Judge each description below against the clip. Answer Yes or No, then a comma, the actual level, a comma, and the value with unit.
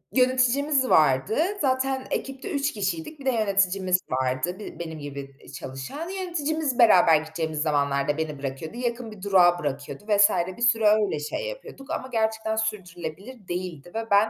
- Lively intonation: Yes, wide, 8.4 semitones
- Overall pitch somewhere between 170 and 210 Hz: Yes, high, 200 Hz